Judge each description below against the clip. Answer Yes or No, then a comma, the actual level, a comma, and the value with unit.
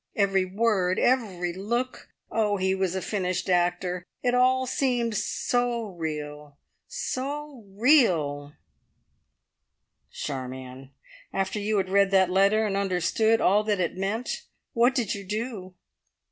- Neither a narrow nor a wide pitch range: Yes, average, 4.3 semitones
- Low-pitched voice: No, high, 195 Hz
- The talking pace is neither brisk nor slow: No, slow, 130 wpm